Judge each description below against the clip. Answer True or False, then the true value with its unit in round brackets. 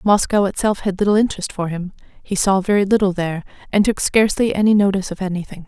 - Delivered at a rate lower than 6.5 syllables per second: False (6.8 syllables/s)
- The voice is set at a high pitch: True (195 Hz)